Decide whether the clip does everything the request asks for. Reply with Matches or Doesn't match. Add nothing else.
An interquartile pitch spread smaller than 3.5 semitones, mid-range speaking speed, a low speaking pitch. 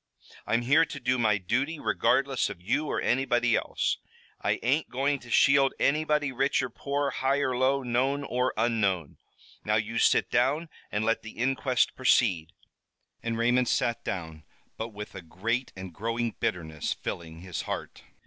Doesn't match